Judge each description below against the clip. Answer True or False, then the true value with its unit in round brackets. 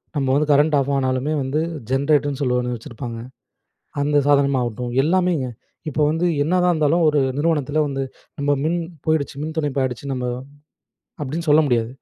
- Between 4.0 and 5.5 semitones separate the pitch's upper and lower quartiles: False (3.0 semitones)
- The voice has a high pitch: False (145 Hz)